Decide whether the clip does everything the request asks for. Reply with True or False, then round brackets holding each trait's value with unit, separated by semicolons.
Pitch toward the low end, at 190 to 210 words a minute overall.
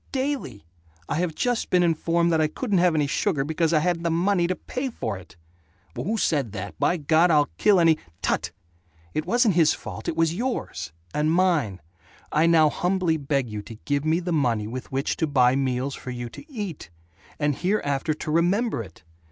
False (160 Hz; 200 wpm)